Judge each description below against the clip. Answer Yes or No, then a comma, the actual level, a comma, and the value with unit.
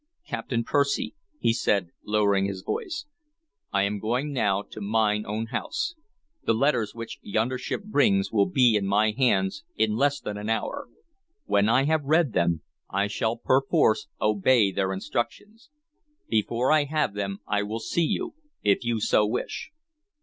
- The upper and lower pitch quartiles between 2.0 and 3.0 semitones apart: No, average, 4.8 semitones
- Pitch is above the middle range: No, low, 110 Hz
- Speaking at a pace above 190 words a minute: No, average, 160 wpm